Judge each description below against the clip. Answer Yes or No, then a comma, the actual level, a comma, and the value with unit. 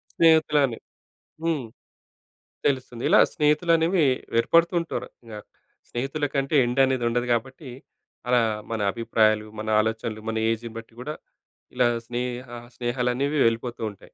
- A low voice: Yes, low, 125 Hz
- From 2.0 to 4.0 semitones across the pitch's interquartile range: No, average, 4.4 semitones